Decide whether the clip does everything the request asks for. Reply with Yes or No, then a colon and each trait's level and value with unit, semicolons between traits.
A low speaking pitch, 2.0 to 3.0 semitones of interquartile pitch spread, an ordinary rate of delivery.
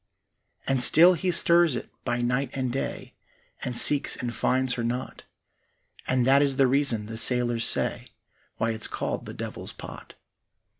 Yes: low, 130 Hz; narrow, 2.5 semitones; average, 160 wpm